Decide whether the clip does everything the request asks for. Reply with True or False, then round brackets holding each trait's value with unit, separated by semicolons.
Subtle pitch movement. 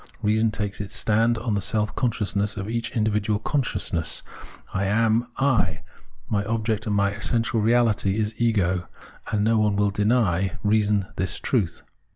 True (2.1 semitones)